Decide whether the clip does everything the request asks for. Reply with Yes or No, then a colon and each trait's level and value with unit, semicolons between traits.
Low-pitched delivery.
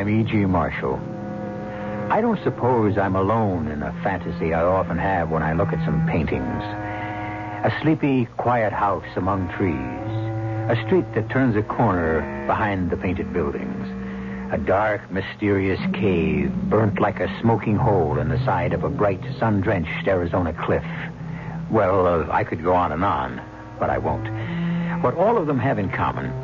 Yes: low, 105 Hz